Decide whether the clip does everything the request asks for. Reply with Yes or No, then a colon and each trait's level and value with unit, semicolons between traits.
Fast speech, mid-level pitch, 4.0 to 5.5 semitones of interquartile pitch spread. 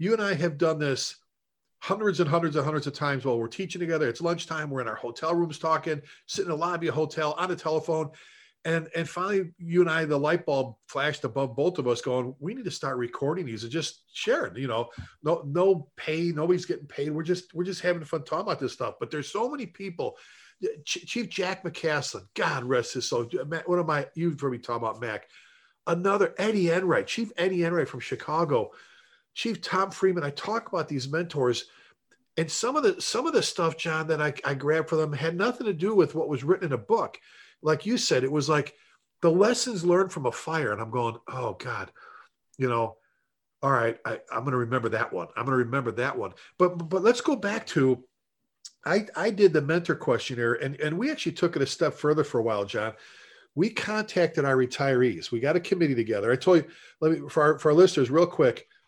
Yes: fast, 225 wpm; medium, 160 Hz; average, 4.6 semitones